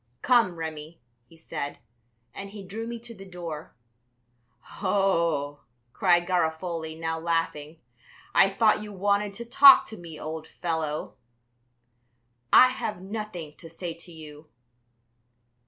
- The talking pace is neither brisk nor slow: No, slow, 125 wpm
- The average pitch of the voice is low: No, medium, 175 Hz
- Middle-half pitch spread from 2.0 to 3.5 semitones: No, average, 4.0 semitones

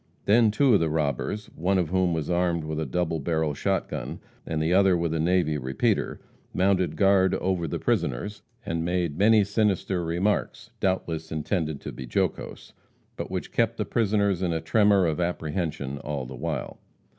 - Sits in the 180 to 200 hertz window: No, very low, 85 Hz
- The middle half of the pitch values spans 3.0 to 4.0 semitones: Yes, average, 3.6 semitones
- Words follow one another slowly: No, average, 180 wpm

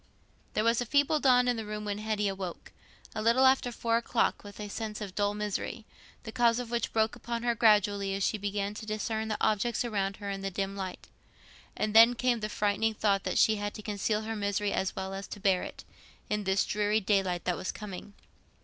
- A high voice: Yes, high, 210 Hz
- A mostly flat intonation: Yes, narrow, 2.2 semitones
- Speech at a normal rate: No, fast, 220 wpm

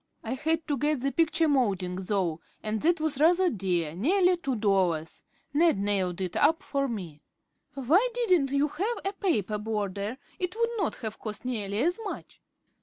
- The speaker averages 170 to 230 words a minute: Yes, average, 175 wpm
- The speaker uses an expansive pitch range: Yes, wide, 8.7 semitones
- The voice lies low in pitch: No, very high, 260 Hz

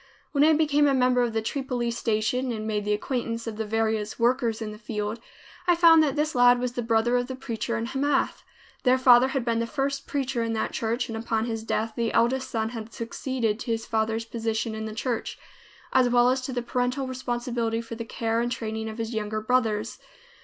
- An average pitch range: No, narrow, 2.3 semitones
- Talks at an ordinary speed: No, fast, 220 wpm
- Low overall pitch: No, high, 235 Hz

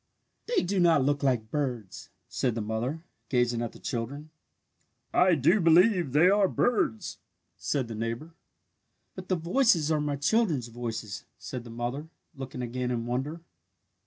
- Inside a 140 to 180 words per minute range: Yes, average, 150 wpm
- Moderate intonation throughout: No, wide, 5.7 semitones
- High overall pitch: No, medium, 140 Hz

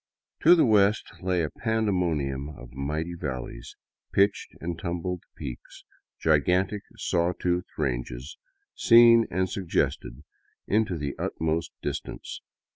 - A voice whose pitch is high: No, very low, 85 Hz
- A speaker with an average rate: No, slow, 115 wpm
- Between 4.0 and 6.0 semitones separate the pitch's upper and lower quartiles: Yes, average, 5.0 semitones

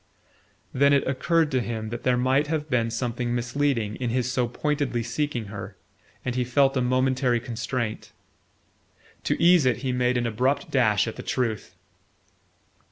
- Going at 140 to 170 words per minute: Yes, average, 165 wpm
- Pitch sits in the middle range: No, low, 125 Hz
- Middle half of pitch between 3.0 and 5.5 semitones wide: No, narrow, 2.4 semitones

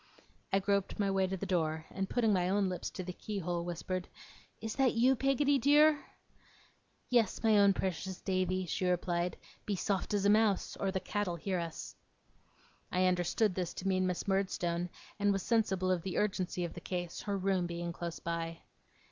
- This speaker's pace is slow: No, average, 190 wpm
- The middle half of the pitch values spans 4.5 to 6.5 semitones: No, narrow, 2.5 semitones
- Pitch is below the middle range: No, high, 190 Hz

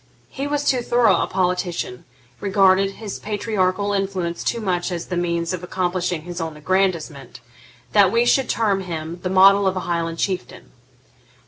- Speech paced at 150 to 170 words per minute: Yes, average, 160 wpm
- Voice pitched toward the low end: No, medium, 185 Hz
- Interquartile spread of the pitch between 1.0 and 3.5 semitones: Yes, narrow, 2.5 semitones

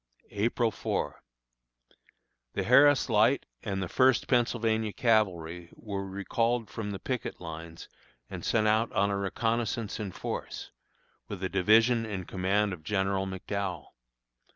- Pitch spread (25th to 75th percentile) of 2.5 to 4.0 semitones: Yes, average, 3.2 semitones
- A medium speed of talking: No, slow, 130 wpm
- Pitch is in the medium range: No, low, 105 Hz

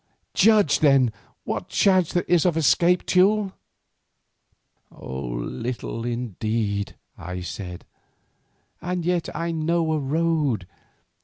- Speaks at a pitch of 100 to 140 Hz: No, medium, 155 Hz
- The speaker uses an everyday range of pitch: No, wide, 8.1 semitones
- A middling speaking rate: No, slow, 100 wpm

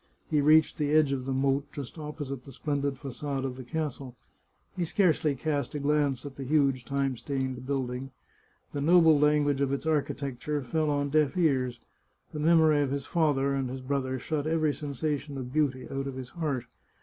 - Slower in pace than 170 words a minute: No, average, 185 wpm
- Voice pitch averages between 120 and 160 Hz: Yes, medium, 140 Hz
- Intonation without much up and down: Yes, narrow, 2.2 semitones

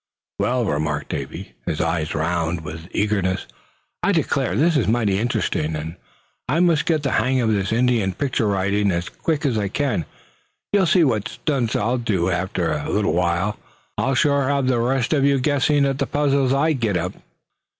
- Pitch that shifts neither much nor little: No, wide, 7.6 semitones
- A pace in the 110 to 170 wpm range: No, average, 180 wpm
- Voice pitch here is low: Yes, low, 115 Hz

